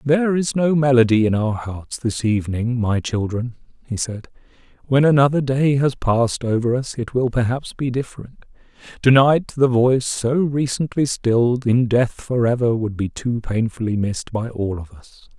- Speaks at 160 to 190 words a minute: Yes, average, 170 wpm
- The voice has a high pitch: No, low, 120 Hz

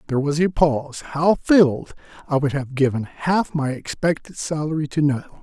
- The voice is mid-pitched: Yes, medium, 150 Hz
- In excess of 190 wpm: No, average, 165 wpm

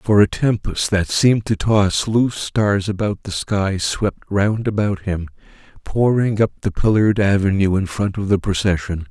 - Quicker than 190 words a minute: No, average, 170 wpm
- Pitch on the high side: No, low, 100 Hz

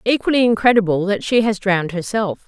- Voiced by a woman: Yes, female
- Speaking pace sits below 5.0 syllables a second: No, 5.9 syllables/s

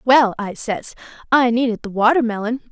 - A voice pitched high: Yes, high, 235 Hz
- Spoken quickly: No, average, 155 wpm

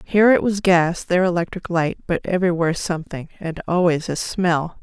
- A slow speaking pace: No, average, 175 wpm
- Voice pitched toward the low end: No, medium, 175 Hz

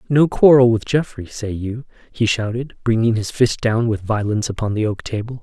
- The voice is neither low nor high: No, low, 115 Hz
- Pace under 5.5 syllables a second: Yes, 5.3 syllables/s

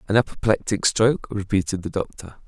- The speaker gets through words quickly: No, average, 145 wpm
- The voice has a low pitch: Yes, low, 105 Hz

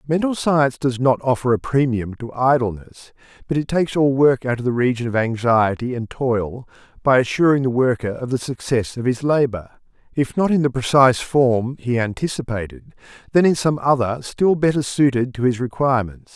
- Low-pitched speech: Yes, low, 130 Hz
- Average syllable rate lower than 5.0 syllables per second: No, 5.3 syllables/s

